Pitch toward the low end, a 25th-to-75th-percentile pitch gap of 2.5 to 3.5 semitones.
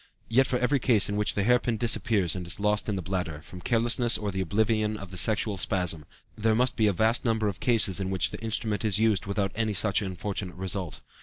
Yes: low, 105 Hz; average, 3.0 semitones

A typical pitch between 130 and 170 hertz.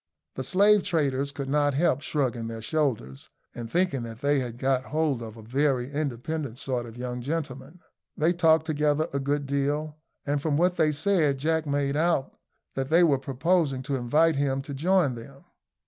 Yes: medium, 140 Hz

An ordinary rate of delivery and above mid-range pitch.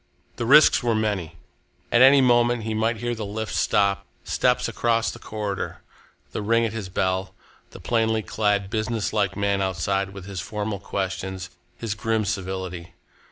No: average, 160 wpm; low, 105 Hz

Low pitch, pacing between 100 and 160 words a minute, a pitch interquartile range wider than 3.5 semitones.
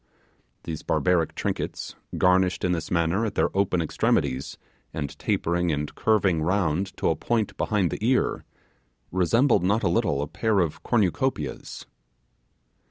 Yes: very low, 90 Hz; average, 140 wpm; average, 4.0 semitones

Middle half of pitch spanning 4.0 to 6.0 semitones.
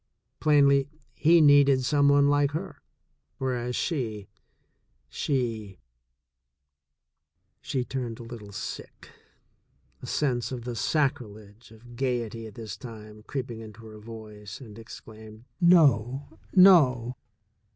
Yes: average, 4.3 semitones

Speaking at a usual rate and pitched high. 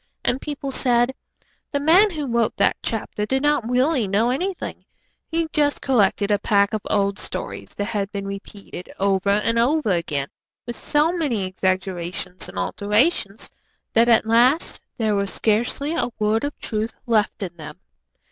Yes: average, 160 wpm; high, 225 Hz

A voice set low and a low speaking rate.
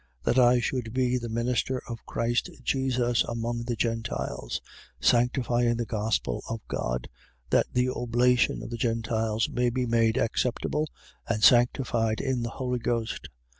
No: low, 120 Hz; average, 145 wpm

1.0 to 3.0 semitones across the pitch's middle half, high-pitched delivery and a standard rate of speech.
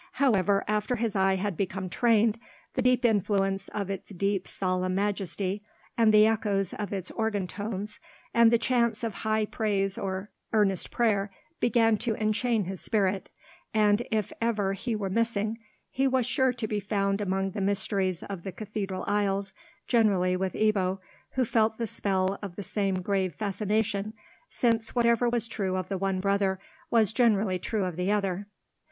Yes: narrow, 2.5 semitones; high, 205 Hz; average, 170 wpm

